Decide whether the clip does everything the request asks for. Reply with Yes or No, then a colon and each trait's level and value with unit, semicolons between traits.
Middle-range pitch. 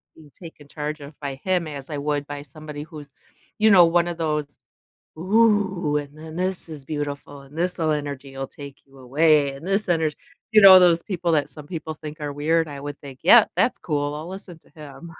Yes: medium, 150 Hz